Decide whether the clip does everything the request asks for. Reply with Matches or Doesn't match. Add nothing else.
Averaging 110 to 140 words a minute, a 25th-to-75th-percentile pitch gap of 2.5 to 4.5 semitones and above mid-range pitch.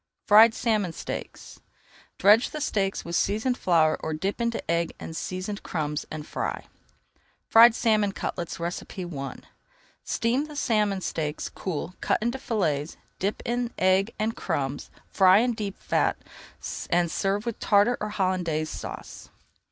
Doesn't match